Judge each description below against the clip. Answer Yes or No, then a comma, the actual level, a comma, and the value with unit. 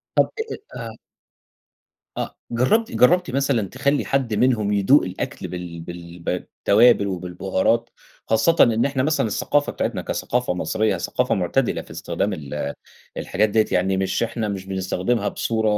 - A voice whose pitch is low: Yes, low, 110 Hz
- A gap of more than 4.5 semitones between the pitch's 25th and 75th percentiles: Yes, average, 5.0 semitones